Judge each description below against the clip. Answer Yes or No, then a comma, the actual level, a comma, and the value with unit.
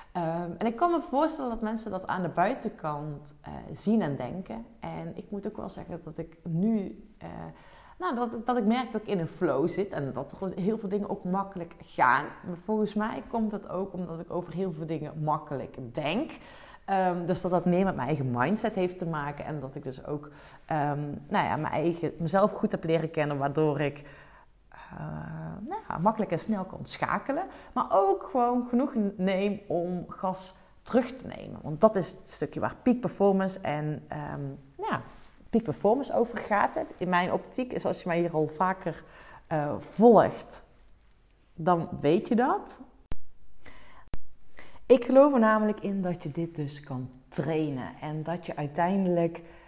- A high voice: No, medium, 180 Hz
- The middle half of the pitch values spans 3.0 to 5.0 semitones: No, wide, 5.5 semitones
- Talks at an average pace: Yes, average, 185 wpm